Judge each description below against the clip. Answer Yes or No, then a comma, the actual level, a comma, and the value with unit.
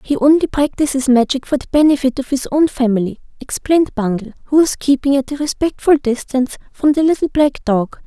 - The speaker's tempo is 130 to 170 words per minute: No, average, 185 wpm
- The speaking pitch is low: No, very high, 270 Hz